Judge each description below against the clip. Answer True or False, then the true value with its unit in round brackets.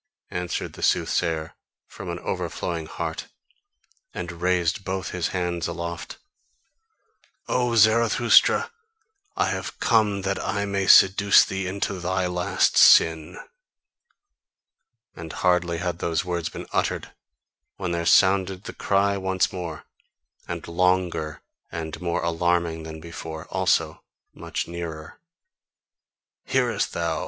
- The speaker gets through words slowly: True (115 wpm)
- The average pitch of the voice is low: True (90 Hz)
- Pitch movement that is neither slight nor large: False (2.2 semitones)